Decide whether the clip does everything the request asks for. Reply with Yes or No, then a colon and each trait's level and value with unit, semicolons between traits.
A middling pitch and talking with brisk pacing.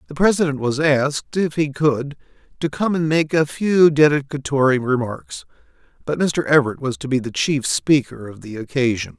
No: medium, 145 Hz; average, 175 wpm